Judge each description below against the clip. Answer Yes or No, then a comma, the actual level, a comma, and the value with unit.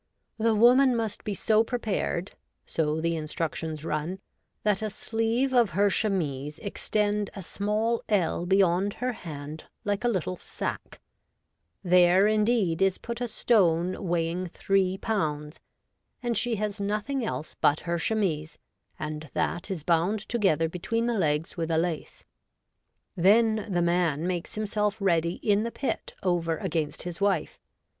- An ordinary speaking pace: Yes, average, 150 wpm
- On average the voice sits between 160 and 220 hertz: Yes, high, 190 Hz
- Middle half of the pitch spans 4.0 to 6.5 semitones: Yes, average, 4.5 semitones